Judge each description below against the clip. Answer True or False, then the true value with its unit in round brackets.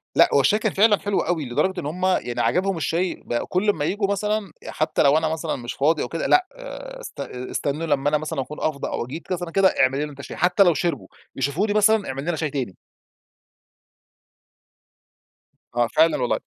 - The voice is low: False (165 Hz)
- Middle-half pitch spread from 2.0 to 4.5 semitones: False (5.4 semitones)